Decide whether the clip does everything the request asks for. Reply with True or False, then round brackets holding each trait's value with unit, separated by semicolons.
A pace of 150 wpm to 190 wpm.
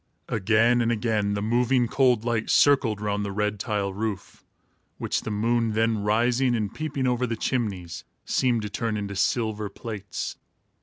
True (160 wpm)